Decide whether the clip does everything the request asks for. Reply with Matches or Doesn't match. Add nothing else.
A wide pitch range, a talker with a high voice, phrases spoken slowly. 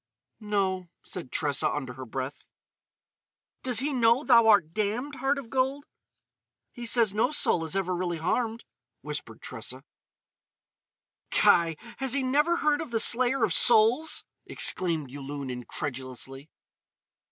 Matches